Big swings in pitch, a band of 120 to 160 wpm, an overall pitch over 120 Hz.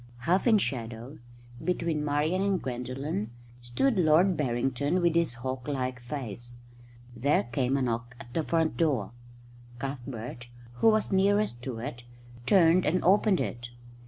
Yes: wide, 5.9 semitones; average, 140 wpm; medium, 140 Hz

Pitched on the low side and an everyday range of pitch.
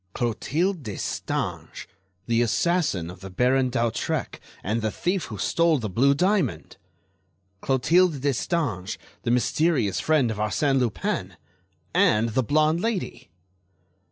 No: low, 130 Hz; wide, 6.8 semitones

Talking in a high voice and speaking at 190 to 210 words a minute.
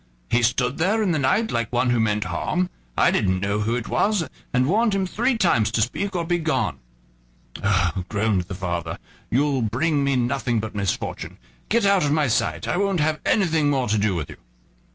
No: low, 125 Hz; average, 200 wpm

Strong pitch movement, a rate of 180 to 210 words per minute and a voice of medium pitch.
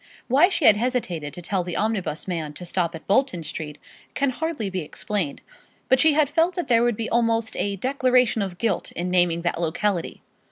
No: wide, 6.5 semitones; average, 200 wpm; high, 205 Hz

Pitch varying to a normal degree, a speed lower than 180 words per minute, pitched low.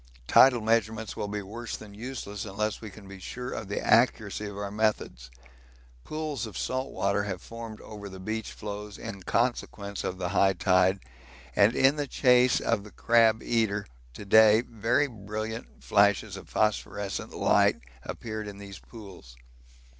No: narrow, 2.3 semitones; average, 160 wpm; low, 105 Hz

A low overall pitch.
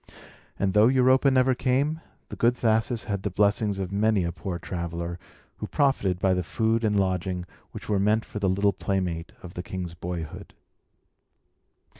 Yes: low, 100 Hz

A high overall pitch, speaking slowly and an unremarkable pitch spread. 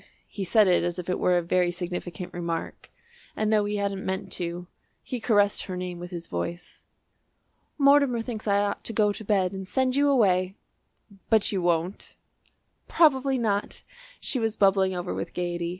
No: high, 195 Hz; average, 180 wpm; average, 3.6 semitones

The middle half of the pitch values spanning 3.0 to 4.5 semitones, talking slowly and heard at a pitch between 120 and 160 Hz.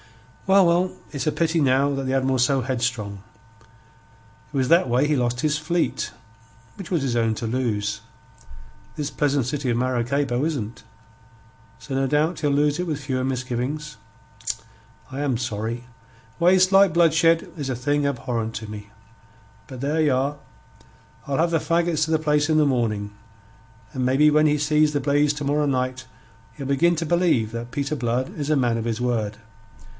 No: average, 3.6 semitones; average, 180 wpm; medium, 140 Hz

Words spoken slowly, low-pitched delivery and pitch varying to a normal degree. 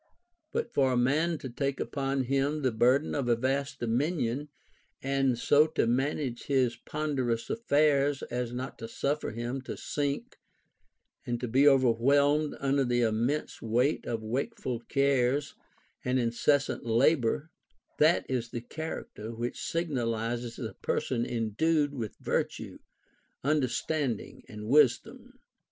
Yes: slow, 130 wpm; low, 130 Hz; average, 3.3 semitones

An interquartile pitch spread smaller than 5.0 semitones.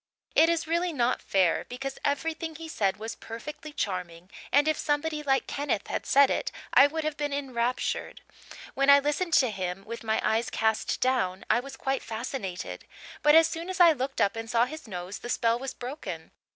No: average, 5.3 semitones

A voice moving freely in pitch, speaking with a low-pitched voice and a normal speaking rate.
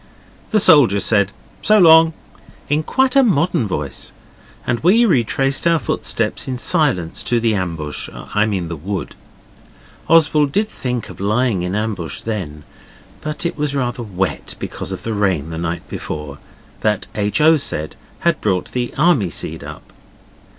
Yes: wide, 8.5 semitones; low, 115 Hz; average, 160 wpm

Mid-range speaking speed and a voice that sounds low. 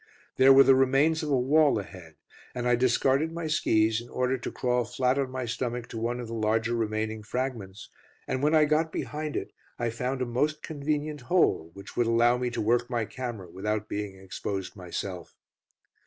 Yes: average, 195 wpm; low, 120 Hz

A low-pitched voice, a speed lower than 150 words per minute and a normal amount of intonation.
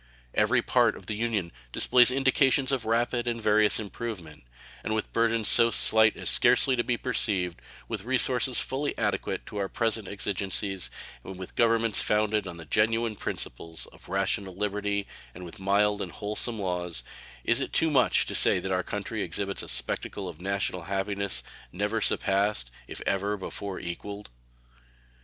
No: low, 105 Hz; average, 160 wpm; average, 3.2 semitones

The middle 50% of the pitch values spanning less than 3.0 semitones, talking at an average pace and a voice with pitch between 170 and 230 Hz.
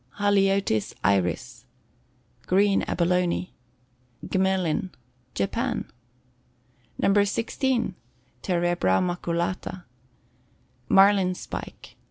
No: narrow, 2.5 semitones; slow, 60 wpm; medium, 185 Hz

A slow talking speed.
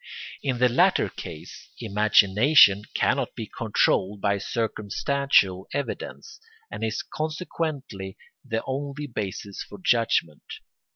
Yes: slow, 105 wpm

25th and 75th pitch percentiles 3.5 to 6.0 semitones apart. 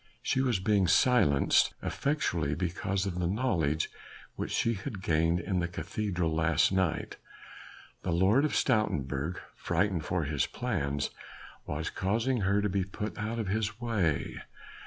Yes: average, 4.5 semitones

